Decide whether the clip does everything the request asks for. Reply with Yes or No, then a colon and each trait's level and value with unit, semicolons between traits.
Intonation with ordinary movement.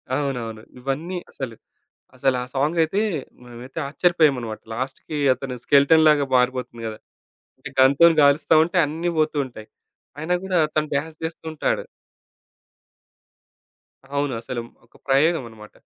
Yes: average, 4.1 semitones